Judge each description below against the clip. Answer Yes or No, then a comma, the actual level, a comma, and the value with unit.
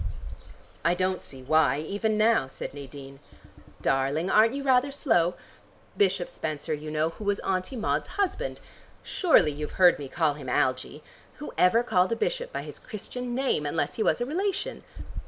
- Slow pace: No, average, 170 wpm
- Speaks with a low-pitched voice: No, medium, 185 Hz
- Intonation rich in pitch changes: Yes, wide, 8.6 semitones